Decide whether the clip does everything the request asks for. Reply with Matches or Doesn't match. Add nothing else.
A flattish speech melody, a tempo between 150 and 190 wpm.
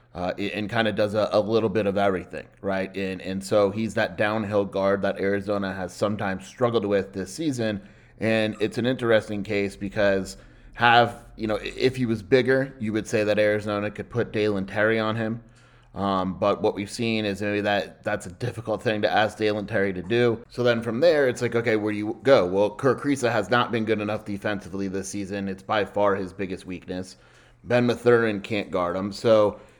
Doesn't match